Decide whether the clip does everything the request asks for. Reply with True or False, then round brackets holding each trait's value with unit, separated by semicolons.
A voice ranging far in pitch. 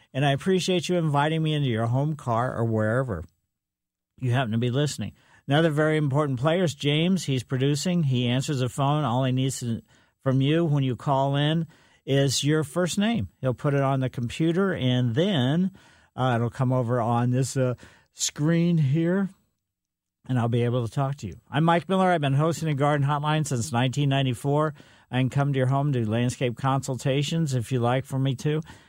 False (3.6 semitones)